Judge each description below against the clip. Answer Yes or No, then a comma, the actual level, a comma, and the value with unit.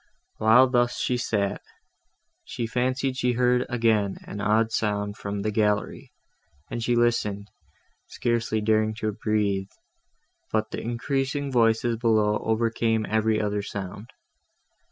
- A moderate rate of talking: No, slow, 125 wpm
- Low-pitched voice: Yes, low, 110 Hz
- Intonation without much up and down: Yes, narrow, 2.3 semitones